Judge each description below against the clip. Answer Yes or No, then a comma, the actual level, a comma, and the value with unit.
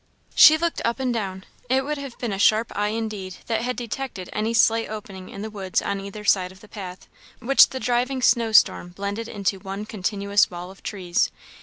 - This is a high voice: Yes, high, 210 Hz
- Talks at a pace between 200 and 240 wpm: Yes, fast, 205 wpm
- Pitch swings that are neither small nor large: Yes, average, 3.4 semitones